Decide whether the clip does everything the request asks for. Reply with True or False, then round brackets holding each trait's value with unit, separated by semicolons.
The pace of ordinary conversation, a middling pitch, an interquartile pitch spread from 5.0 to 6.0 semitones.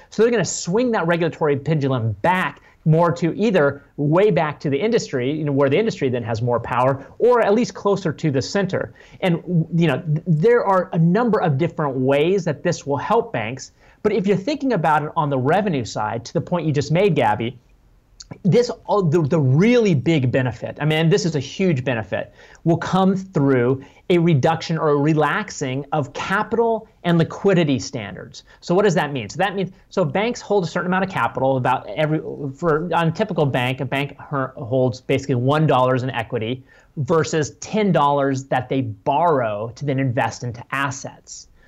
True (185 wpm; 155 Hz; 5.4 semitones)